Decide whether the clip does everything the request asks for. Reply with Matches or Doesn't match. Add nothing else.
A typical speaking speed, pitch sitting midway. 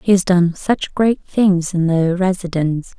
Matches